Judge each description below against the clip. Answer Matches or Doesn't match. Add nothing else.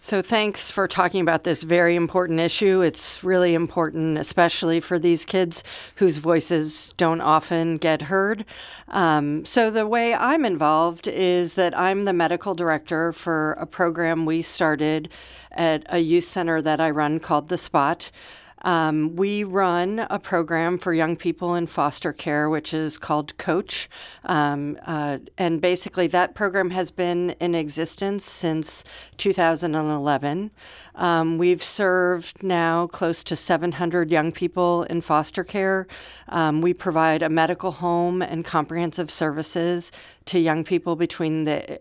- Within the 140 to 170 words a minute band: Matches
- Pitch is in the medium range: Matches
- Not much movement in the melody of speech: Matches